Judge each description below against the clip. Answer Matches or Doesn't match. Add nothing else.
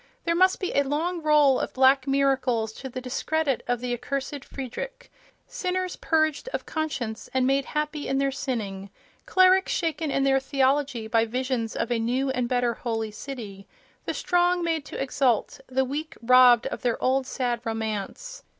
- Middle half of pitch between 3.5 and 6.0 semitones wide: Matches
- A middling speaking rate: Matches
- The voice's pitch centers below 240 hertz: Doesn't match